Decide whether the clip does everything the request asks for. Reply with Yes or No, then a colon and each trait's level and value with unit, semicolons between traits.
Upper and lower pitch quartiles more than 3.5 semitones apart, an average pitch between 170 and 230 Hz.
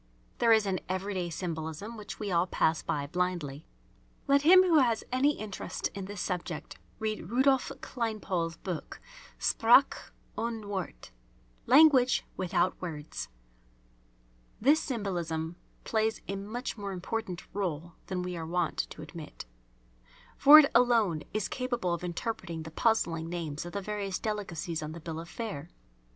Yes: average, 5.1 semitones; high, 190 Hz